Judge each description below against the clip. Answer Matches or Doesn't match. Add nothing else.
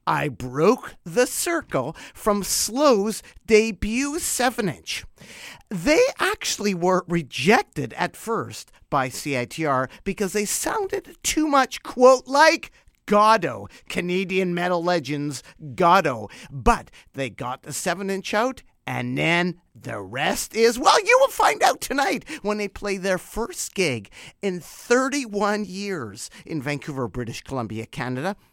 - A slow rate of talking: Matches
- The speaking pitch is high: Matches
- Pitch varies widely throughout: Matches